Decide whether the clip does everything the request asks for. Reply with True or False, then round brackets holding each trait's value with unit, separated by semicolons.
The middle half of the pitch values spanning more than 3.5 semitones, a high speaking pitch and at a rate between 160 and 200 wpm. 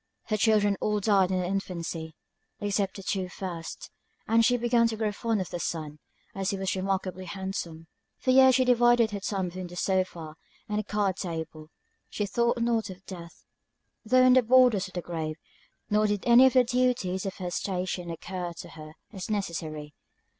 True (4.1 semitones; 195 Hz; 190 wpm)